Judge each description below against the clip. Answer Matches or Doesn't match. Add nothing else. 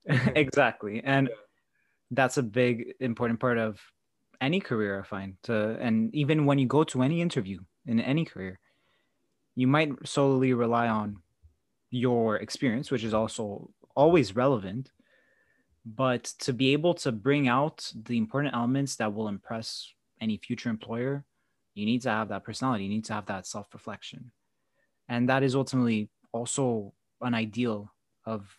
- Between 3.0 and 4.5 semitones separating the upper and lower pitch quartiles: Matches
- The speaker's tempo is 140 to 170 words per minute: Matches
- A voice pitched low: Matches